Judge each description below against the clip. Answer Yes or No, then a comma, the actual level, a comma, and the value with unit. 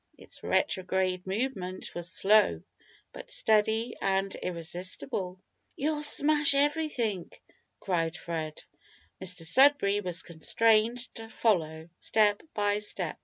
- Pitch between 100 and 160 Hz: No, high, 195 Hz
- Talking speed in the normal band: No, slow, 105 wpm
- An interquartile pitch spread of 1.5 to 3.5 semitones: No, average, 4.1 semitones